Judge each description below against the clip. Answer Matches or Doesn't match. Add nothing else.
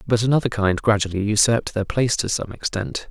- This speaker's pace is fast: Doesn't match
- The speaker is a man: Matches